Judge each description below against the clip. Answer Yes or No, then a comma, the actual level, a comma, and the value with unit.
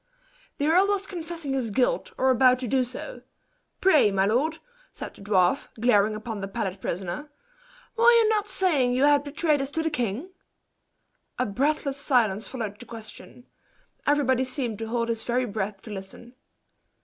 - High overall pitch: Yes, very high, 255 Hz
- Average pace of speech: Yes, average, 170 wpm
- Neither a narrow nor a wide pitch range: No, wide, 5.7 semitones